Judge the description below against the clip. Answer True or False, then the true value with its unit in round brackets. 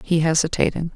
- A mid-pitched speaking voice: True (165 Hz)